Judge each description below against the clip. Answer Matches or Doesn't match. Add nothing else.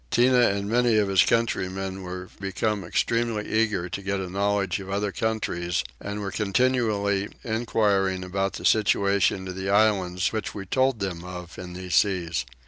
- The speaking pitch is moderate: Doesn't match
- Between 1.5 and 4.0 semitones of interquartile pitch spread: Matches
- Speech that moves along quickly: Doesn't match